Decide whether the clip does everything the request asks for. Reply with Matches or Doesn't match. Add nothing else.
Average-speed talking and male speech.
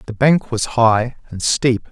Matches